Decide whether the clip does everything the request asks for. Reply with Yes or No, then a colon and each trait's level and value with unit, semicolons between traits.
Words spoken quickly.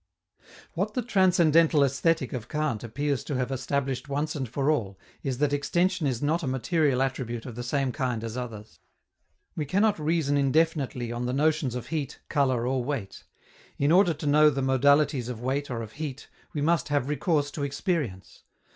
No: average, 180 wpm